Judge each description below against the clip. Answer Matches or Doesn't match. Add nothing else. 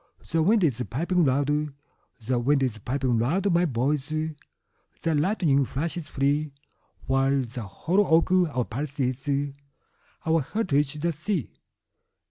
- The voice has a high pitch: Doesn't match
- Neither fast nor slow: Doesn't match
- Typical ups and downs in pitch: Matches